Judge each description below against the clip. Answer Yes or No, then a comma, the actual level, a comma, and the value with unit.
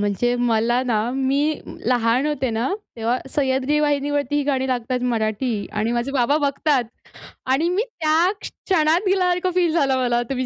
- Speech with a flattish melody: No, average, 3.8 semitones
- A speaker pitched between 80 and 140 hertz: No, very high, 265 Hz